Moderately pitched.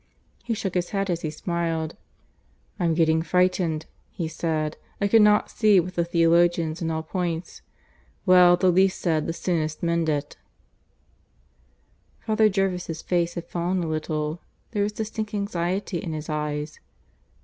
Yes: medium, 170 Hz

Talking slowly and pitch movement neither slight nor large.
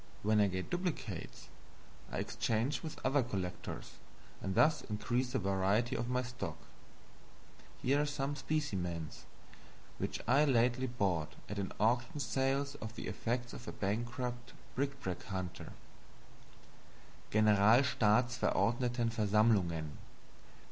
Yes: slow, 115 wpm; average, 4.3 semitones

